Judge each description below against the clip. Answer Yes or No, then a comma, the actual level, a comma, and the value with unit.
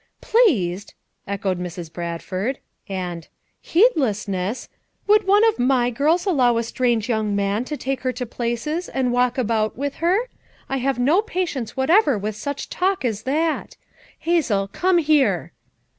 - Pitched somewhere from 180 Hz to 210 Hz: No, very high, 250 Hz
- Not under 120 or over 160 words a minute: Yes, average, 155 wpm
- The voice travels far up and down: Yes, wide, 7.2 semitones